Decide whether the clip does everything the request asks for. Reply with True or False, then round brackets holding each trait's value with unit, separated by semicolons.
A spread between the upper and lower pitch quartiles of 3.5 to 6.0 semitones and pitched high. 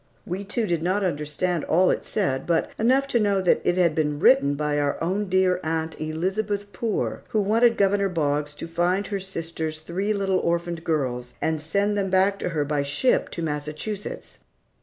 False (4.3 semitones; 175 Hz)